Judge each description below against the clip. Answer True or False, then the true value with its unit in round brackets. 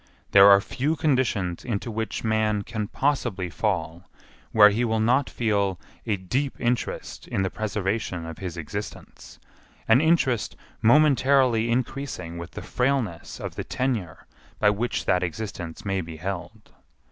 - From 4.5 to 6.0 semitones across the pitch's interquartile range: True (4.8 semitones)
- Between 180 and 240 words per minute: False (145 wpm)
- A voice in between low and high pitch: False (110 Hz)